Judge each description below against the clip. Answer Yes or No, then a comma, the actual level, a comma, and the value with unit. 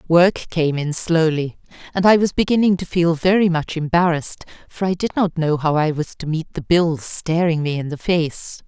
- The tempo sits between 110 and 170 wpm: No, fast, 205 wpm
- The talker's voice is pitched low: No, medium, 165 Hz